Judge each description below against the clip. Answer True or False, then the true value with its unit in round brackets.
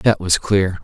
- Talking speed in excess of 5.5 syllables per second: False (4.0 syllables/s)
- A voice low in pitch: True (95 Hz)